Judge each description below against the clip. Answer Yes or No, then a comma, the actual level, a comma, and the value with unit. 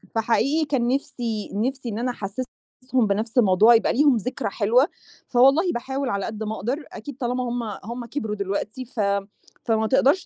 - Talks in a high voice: Yes, high, 240 Hz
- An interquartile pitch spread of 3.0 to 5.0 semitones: Yes, average, 3.3 semitones